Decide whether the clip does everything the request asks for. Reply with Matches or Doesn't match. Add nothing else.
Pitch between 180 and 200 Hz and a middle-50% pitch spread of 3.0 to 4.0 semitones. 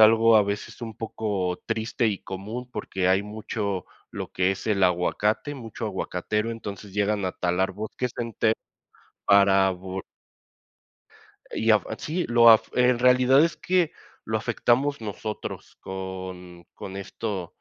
Doesn't match